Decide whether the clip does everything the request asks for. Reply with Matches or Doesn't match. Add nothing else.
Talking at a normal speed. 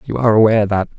Doesn't match